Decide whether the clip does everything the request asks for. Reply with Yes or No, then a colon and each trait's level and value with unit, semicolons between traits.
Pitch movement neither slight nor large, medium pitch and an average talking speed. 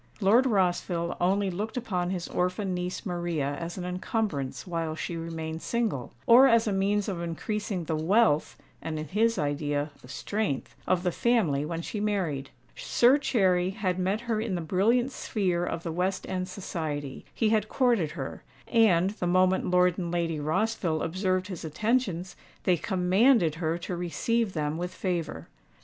Yes: average, 4.1 semitones; medium, 180 Hz; average, 165 wpm